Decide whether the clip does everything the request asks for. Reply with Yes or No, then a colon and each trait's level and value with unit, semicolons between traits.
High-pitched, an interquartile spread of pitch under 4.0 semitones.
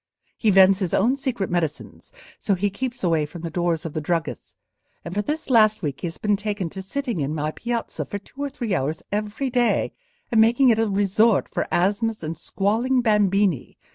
No: high, 205 Hz; average, 4.9 semitones